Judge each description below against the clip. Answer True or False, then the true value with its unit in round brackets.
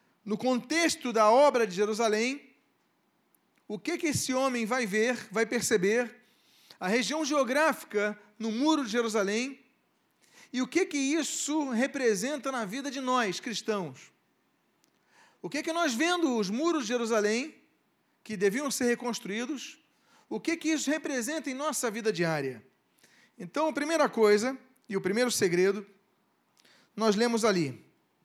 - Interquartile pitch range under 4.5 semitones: False (5.0 semitones)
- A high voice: True (245 Hz)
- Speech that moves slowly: False (140 wpm)